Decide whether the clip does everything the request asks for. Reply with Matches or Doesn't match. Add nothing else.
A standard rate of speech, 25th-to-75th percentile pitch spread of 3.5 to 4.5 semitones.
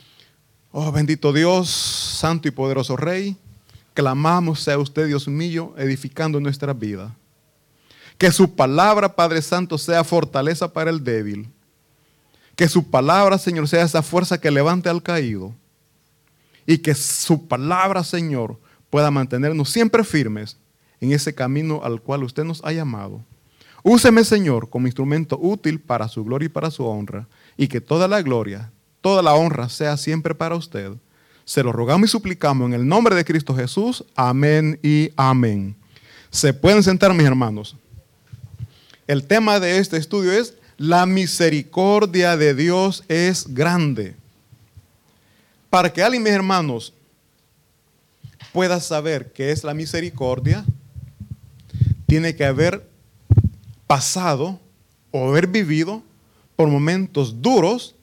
Doesn't match